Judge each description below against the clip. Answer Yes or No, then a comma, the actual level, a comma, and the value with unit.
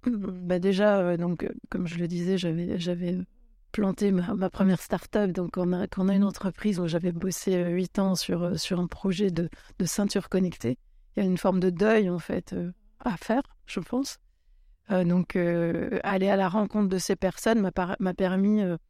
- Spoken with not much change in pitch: Yes, narrow, 2.3 semitones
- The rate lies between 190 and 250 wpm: Yes, average, 215 wpm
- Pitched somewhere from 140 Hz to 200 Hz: Yes, high, 190 Hz